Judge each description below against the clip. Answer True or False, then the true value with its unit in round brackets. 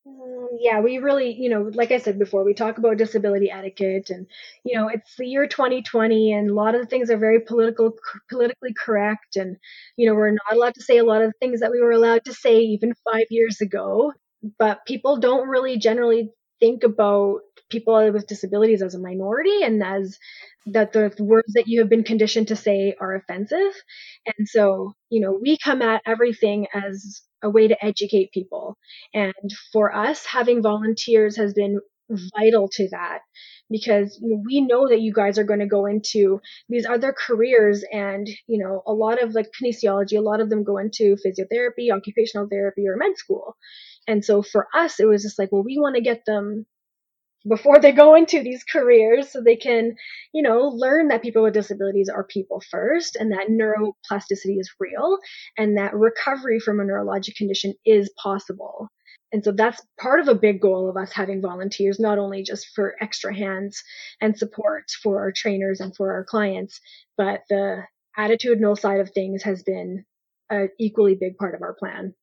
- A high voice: True (215 Hz)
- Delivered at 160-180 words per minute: False (190 wpm)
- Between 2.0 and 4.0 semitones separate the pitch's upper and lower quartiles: True (2.5 semitones)